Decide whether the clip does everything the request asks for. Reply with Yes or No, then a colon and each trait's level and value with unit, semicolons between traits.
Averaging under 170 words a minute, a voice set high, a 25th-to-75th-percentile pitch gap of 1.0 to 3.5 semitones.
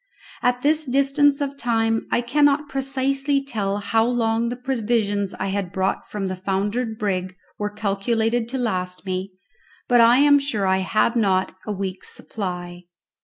No: average, 160 wpm; high, 225 Hz; average, 4.9 semitones